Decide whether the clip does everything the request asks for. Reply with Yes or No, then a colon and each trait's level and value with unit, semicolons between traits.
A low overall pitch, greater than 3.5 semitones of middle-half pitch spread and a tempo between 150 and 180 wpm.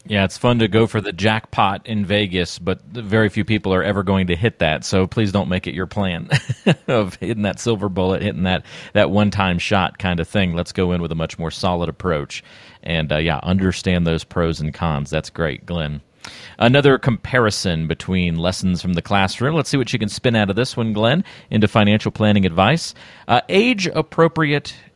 No: low, 100 Hz; average, 4.0 semitones; fast, 205 wpm